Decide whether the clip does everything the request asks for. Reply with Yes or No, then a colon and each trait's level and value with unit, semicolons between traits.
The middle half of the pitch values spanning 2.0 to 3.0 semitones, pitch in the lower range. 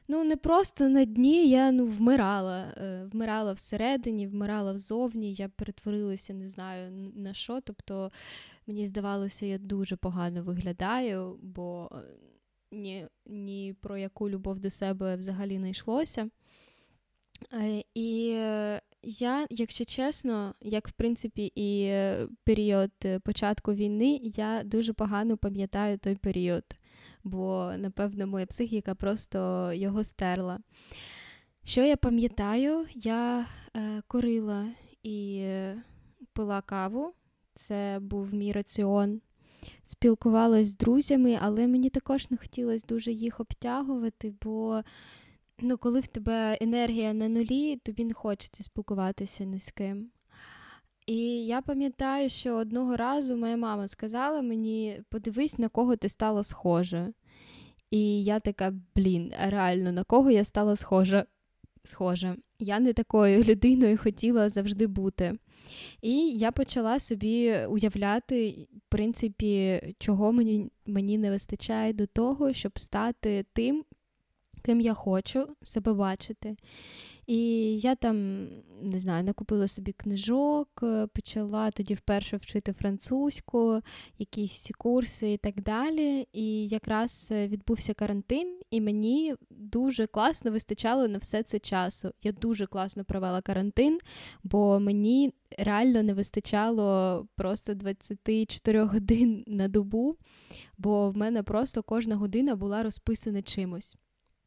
No: average, 2.7 semitones; high, 215 Hz